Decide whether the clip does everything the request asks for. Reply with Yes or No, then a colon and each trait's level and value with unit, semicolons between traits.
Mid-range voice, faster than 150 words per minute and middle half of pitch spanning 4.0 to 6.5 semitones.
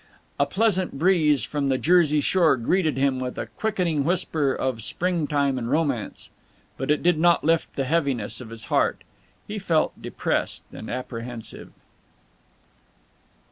No: medium, 150 Hz; average, 140 wpm; average, 4.9 semitones